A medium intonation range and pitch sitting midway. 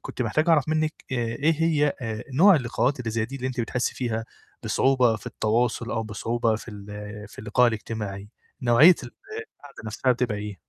No: average, 3.3 semitones; low, 120 Hz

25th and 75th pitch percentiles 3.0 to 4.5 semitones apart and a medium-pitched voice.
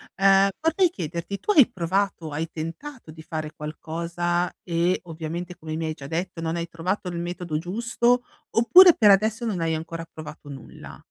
Yes: average, 3.7 semitones; medium, 175 Hz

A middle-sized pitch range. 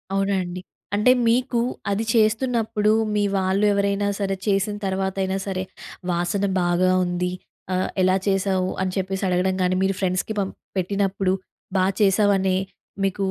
No: narrow, 1.5 semitones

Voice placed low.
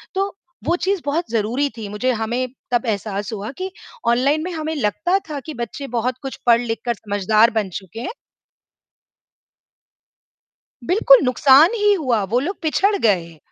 No: very high, 250 Hz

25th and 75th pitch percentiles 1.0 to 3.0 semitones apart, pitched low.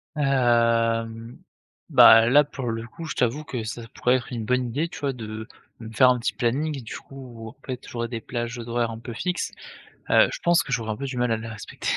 Yes: narrow, 2.6 semitones; low, 120 Hz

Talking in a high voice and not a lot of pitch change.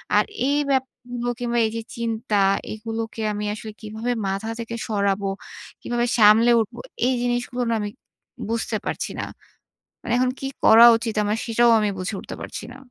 Yes: high, 225 Hz; narrow, 2.1 semitones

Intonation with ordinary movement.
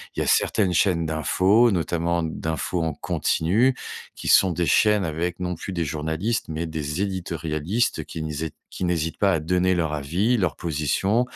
Yes: average, 3.2 semitones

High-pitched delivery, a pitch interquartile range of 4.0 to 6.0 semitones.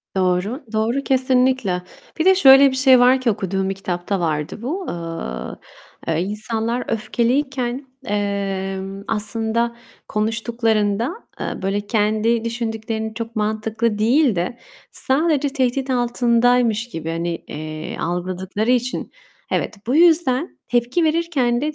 Yes: high, 230 Hz; average, 4.3 semitones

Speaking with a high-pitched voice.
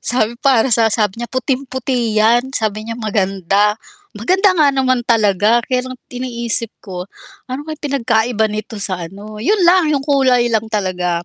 Yes: high, 235 Hz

